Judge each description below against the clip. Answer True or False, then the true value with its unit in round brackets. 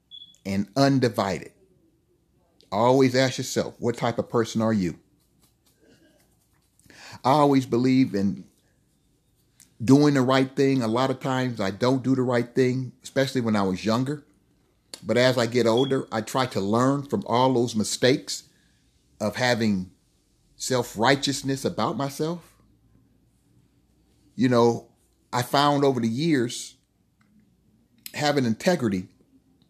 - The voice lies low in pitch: True (125 Hz)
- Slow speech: True (125 wpm)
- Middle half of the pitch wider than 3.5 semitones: False (3.2 semitones)